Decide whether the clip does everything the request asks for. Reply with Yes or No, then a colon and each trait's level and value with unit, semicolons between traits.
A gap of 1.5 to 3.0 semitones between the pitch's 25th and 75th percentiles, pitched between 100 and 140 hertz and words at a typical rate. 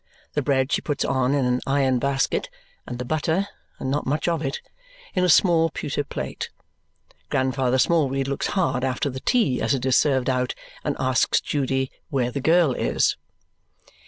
Yes: narrow, 2.5 semitones; low, 135 Hz; average, 175 wpm